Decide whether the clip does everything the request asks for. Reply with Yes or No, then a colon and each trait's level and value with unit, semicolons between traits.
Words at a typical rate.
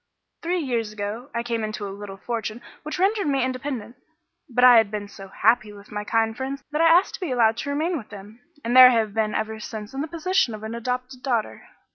No: fast, 235 wpm